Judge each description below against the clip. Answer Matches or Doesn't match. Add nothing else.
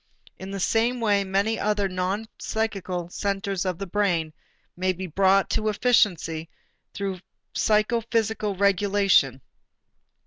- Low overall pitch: Doesn't match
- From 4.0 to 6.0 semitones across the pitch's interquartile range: Doesn't match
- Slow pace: Matches